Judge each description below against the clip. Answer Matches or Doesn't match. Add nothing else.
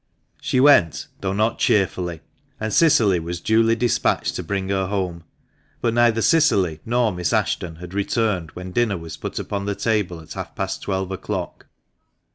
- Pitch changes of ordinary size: Matches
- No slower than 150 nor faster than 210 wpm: Matches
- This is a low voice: Matches